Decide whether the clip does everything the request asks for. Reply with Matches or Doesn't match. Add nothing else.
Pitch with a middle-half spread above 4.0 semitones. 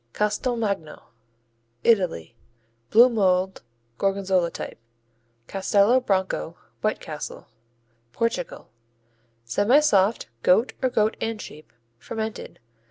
Doesn't match